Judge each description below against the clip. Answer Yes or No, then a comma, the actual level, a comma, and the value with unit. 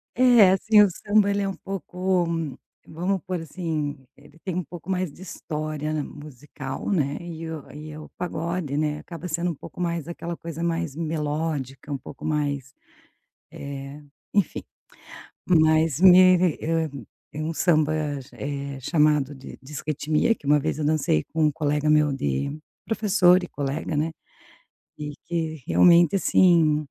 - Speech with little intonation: No, average, 3.2 semitones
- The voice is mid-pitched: Yes, medium, 155 Hz